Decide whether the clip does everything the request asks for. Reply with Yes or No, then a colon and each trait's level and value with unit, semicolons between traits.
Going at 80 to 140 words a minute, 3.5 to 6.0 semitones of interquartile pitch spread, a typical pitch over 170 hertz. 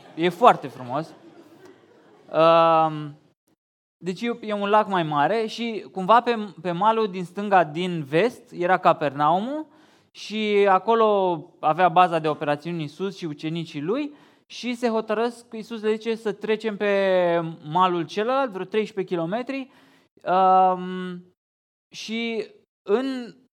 Yes: slow, 115 wpm; average, 5.1 semitones; high, 190 Hz